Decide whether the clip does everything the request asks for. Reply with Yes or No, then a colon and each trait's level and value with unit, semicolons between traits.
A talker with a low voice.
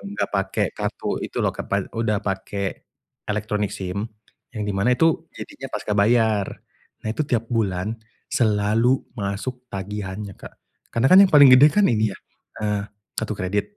Yes: low, 105 Hz